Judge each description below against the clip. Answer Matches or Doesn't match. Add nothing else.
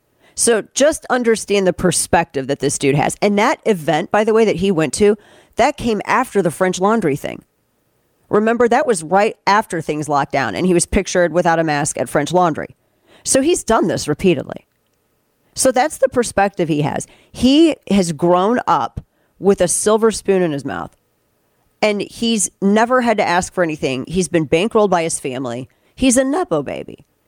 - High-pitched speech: Matches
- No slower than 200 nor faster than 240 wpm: Doesn't match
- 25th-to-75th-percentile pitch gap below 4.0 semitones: Doesn't match